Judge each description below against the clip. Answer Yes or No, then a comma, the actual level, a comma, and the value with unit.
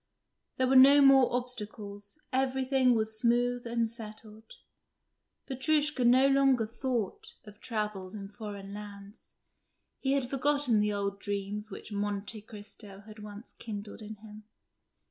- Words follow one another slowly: Yes, slow, 130 wpm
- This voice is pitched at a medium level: No, high, 220 Hz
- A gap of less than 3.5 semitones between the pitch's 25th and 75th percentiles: No, average, 3.9 semitones